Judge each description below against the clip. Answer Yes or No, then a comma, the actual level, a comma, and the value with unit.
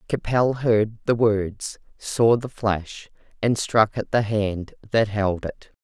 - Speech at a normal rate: Yes, average, 155 wpm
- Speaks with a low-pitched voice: Yes, low, 110 Hz